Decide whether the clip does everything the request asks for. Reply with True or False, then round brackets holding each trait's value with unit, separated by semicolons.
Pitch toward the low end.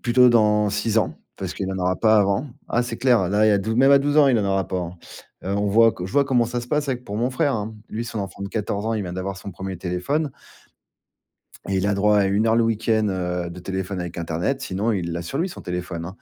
True (105 Hz)